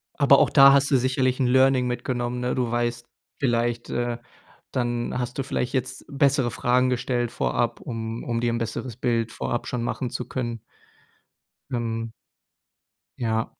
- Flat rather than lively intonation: Yes, narrow, 1.6 semitones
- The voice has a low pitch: Yes, low, 120 Hz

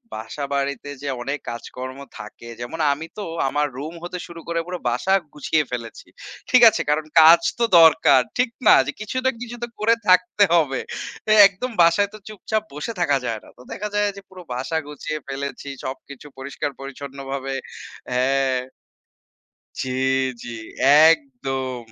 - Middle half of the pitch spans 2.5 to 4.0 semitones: No, average, 4.6 semitones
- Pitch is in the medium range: Yes, medium, 145 Hz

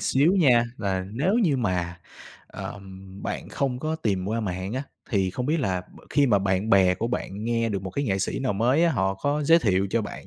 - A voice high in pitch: No, low, 110 Hz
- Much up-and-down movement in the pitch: Yes, wide, 5.9 semitones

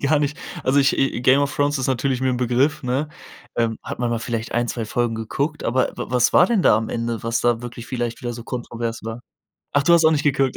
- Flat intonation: No, average, 3.1 semitones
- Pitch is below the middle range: Yes, low, 125 Hz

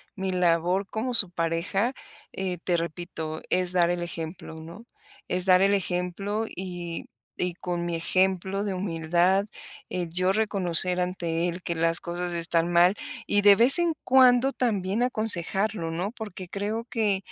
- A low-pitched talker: No, medium, 180 Hz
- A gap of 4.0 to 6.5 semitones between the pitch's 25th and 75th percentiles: No, average, 2.8 semitones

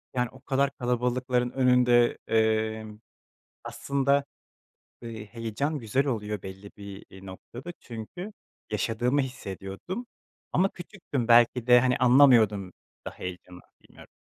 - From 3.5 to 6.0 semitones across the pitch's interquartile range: Yes, average, 3.8 semitones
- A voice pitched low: Yes, low, 120 Hz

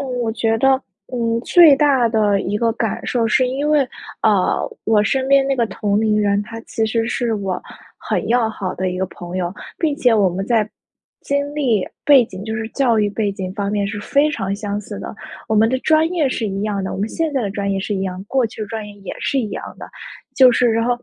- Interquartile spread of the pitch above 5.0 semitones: No, average, 3.9 semitones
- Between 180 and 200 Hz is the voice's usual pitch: No, high, 220 Hz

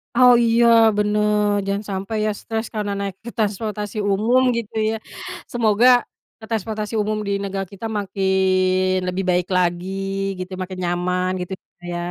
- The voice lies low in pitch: No, high, 200 Hz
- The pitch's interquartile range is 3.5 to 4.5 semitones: No, narrow, 2.5 semitones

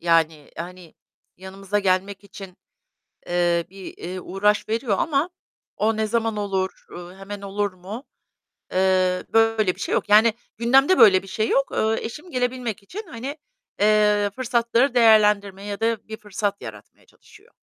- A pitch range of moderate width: Yes, average, 3.2 semitones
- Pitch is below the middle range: No, high, 205 Hz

